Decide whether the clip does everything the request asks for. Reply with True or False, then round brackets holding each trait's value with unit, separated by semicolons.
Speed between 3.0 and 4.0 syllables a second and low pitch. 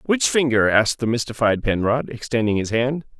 False (5.5 syllables/s; 120 Hz)